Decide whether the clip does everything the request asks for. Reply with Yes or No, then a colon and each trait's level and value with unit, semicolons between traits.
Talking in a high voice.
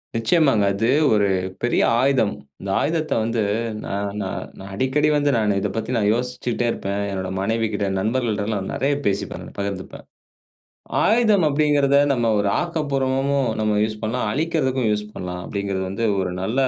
No: low, 115 Hz